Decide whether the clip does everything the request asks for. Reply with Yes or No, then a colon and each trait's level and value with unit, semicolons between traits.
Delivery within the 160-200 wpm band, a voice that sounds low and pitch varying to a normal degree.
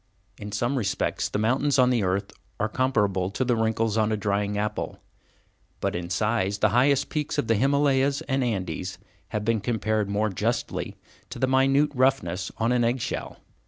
Yes: average, 180 wpm; low, 110 Hz; average, 4.2 semitones